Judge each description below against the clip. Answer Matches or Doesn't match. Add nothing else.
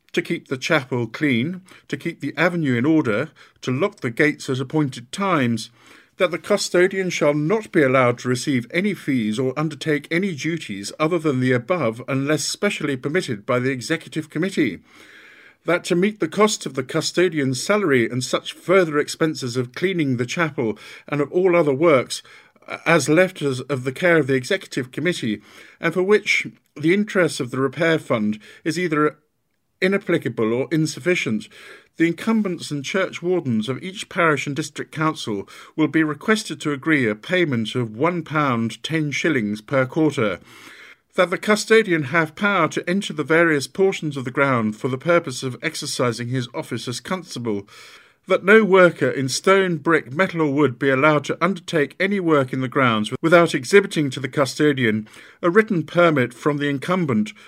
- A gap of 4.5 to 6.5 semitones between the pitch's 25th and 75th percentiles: Matches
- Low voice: Doesn't match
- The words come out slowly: Doesn't match